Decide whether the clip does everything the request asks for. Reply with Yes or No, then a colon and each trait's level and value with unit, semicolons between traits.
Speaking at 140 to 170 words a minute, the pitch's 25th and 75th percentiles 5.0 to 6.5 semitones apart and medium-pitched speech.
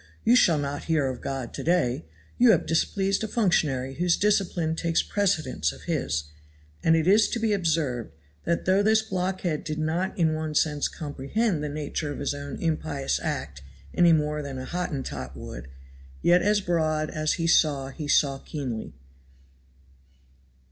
No: average, 165 wpm; average, 4.2 semitones; medium, 155 Hz